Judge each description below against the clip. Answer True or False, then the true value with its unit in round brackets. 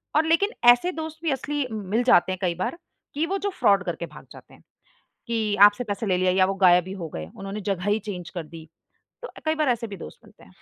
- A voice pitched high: True (205 Hz)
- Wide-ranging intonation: True (8.1 semitones)